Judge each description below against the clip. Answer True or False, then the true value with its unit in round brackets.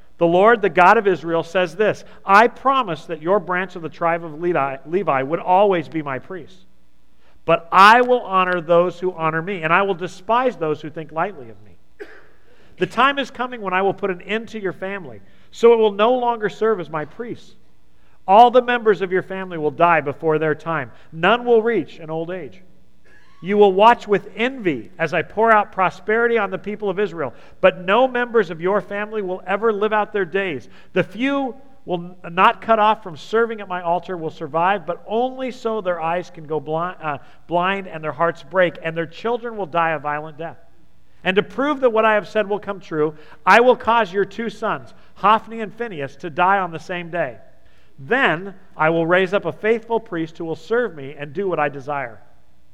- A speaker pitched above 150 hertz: True (185 Hz)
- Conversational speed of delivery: False (210 wpm)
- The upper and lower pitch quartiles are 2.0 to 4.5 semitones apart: False (4.9 semitones)